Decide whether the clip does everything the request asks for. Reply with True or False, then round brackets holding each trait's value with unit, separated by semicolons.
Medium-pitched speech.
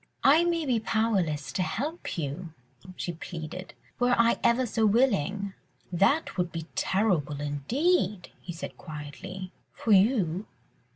False (195 Hz)